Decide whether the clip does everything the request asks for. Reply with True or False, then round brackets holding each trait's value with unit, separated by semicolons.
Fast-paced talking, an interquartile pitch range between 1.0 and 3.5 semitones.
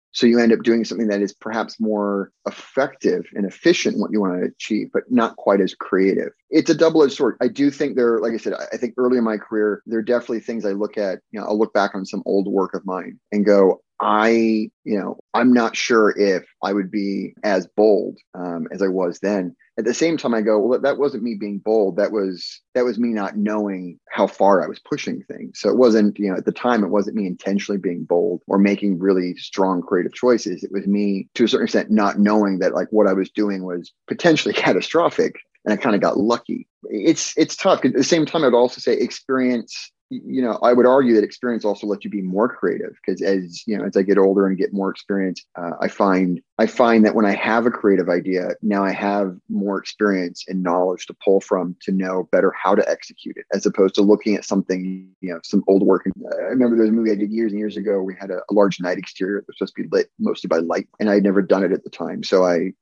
True (250 wpm; 2.7 semitones)